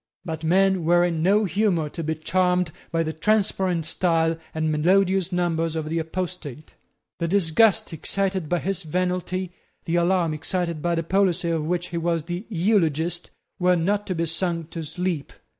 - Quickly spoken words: No, average, 170 wpm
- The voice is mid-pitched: Yes, medium, 175 Hz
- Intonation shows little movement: Yes, narrow, 2.2 semitones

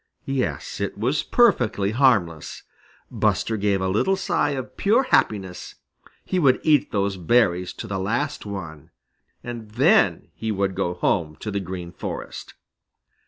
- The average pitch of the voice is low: Yes, low, 105 Hz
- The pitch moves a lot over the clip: Yes, wide, 5.9 semitones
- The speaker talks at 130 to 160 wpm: Yes, average, 145 wpm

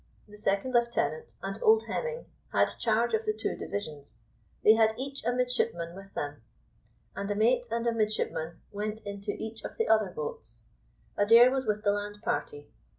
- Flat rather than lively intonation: No, average, 3.4 semitones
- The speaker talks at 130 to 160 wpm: No, average, 175 wpm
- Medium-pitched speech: No, high, 220 Hz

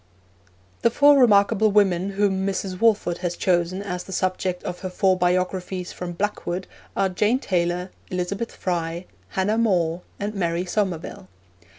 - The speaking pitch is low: No, medium, 185 Hz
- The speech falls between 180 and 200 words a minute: No, average, 145 wpm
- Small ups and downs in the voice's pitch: Yes, narrow, 2.2 semitones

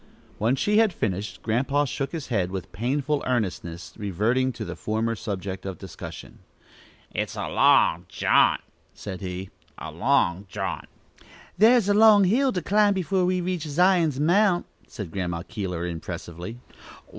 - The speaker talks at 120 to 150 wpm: Yes, average, 145 wpm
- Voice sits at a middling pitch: No, low, 120 Hz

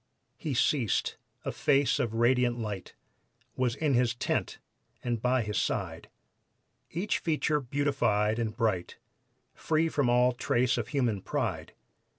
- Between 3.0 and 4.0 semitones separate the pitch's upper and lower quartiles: Yes, average, 3.5 semitones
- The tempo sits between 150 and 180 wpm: No, slow, 135 wpm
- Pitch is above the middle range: No, low, 125 Hz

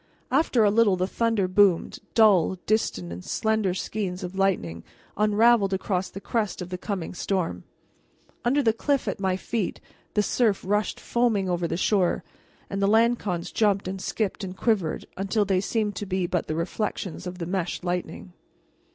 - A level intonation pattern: No, average, 3.0 semitones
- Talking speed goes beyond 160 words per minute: Yes, average, 170 wpm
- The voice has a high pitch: Yes, high, 195 Hz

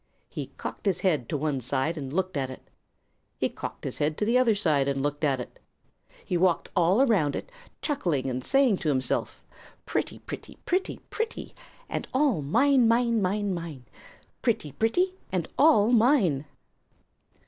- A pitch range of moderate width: No, wide, 8.2 semitones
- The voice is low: No, medium, 185 Hz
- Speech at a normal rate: Yes, average, 165 wpm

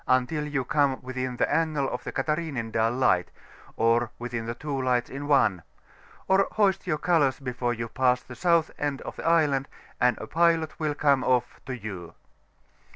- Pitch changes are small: No, average, 3.8 semitones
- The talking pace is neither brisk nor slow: Yes, average, 170 wpm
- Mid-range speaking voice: No, low, 130 Hz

